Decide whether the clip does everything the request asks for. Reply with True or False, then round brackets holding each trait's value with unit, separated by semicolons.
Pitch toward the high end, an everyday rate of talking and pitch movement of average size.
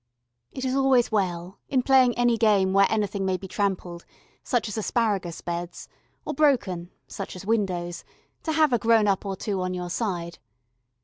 True (200 Hz; 175 wpm; 4.5 semitones)